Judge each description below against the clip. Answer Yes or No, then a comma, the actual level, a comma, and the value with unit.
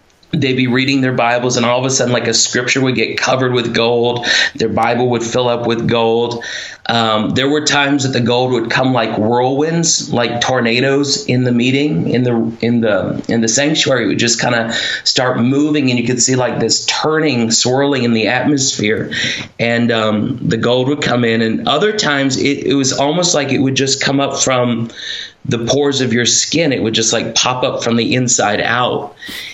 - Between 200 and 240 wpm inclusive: Yes, fast, 205 wpm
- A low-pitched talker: Yes, low, 125 Hz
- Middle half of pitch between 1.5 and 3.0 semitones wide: Yes, average, 2.7 semitones